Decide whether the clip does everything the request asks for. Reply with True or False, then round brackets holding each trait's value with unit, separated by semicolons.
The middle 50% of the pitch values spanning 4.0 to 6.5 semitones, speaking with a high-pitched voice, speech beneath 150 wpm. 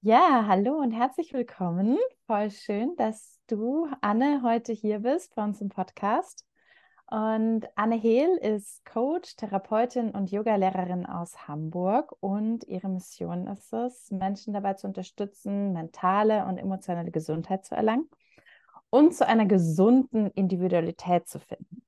True (4.5 semitones; 215 Hz; 135 wpm)